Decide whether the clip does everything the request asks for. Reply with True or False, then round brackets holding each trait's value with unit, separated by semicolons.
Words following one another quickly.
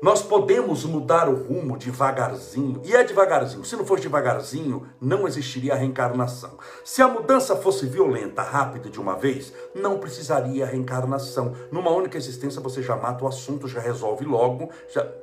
False (160 wpm)